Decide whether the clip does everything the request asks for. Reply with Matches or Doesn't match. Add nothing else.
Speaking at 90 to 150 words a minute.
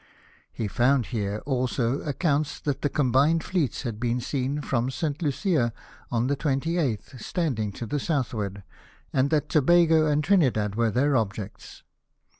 Matches